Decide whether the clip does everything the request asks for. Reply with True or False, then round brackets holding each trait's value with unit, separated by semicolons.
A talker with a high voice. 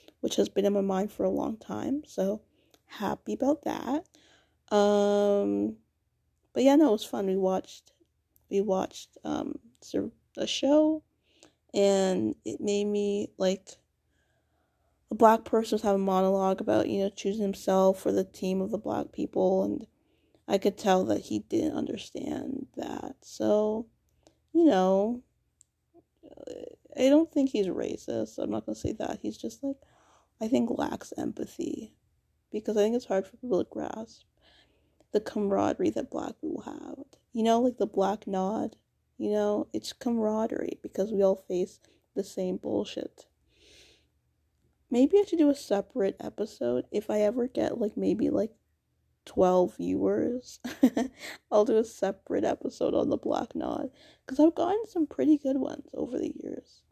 True (220 Hz)